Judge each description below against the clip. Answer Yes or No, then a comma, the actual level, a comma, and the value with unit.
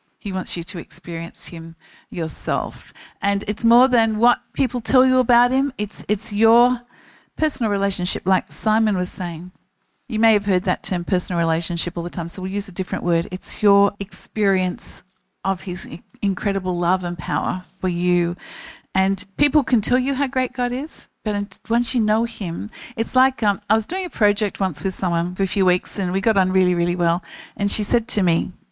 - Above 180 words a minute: Yes, average, 200 wpm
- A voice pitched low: No, high, 200 Hz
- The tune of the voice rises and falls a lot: No, average, 4.3 semitones